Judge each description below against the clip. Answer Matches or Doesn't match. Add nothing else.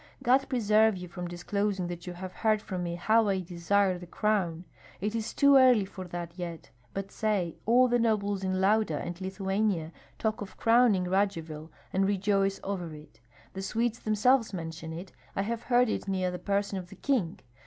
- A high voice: Matches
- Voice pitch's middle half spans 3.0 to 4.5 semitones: Matches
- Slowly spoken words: Doesn't match